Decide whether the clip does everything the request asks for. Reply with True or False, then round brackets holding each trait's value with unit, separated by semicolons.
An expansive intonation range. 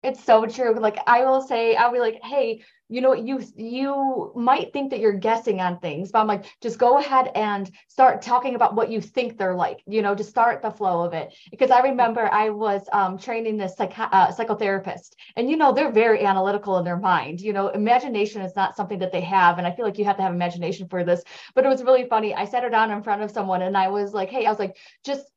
False (4.0 semitones)